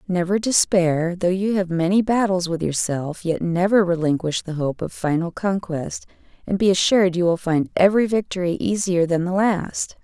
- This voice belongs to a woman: Yes, female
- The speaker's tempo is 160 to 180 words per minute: Yes, average, 175 wpm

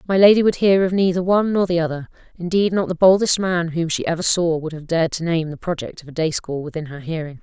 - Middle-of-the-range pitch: Yes, medium, 170 Hz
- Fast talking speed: Yes, fast, 265 wpm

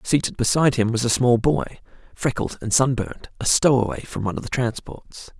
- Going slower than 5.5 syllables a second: No, 5.6 syllables/s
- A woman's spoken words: No, male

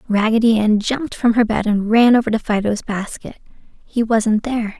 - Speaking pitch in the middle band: No, high, 220 Hz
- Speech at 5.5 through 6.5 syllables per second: No, 5.1 syllables/s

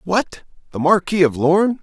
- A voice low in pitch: No, medium, 180 Hz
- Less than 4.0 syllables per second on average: No, 5.6 syllables/s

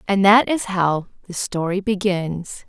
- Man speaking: No, female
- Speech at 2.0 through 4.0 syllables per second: Yes, 3.9 syllables/s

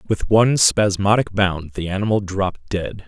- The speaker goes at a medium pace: Yes, average, 155 wpm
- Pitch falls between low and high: No, low, 100 Hz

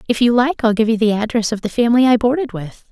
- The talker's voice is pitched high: Yes, high, 230 Hz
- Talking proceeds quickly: Yes, fast, 290 wpm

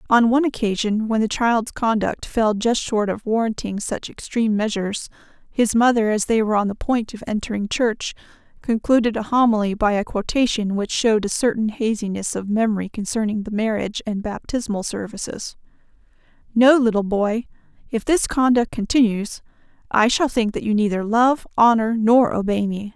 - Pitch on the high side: Yes, high, 220 Hz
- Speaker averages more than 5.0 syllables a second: Yes, 5.2 syllables/s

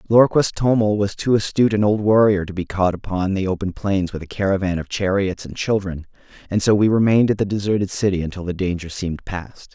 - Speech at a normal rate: No, fast, 215 wpm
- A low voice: Yes, low, 100 Hz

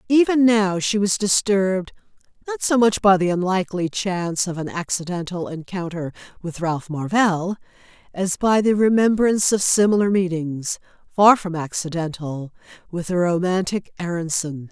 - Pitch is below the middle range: No, medium, 185 Hz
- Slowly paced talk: Yes, slow, 130 wpm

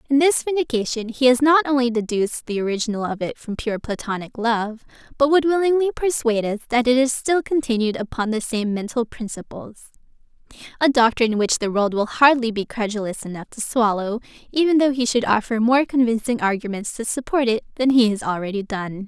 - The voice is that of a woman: Yes, female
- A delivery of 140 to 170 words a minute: No, average, 185 wpm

